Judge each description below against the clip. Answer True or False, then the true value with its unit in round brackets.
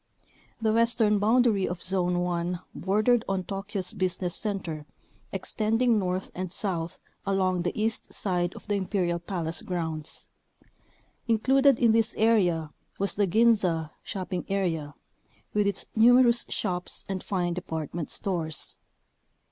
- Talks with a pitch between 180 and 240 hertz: True (190 Hz)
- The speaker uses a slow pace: True (125 wpm)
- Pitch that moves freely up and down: False (3.6 semitones)